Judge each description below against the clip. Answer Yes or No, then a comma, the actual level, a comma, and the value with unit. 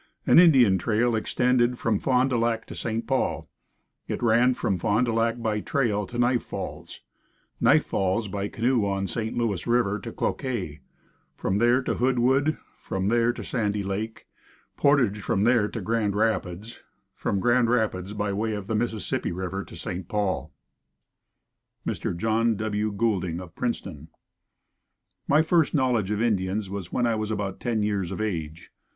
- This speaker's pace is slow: No, average, 165 wpm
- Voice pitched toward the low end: Yes, low, 110 Hz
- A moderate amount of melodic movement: Yes, average, 3.3 semitones